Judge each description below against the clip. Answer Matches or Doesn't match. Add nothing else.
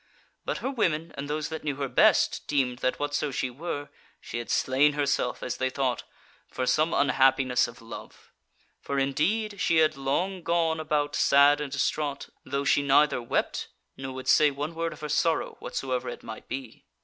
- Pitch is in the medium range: Matches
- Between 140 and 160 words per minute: Doesn't match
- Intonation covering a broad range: Doesn't match